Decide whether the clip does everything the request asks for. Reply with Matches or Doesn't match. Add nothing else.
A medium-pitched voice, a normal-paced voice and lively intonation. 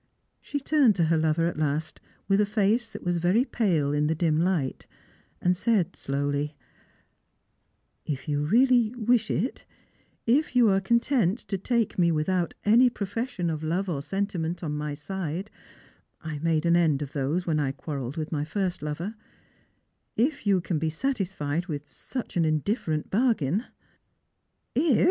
Matches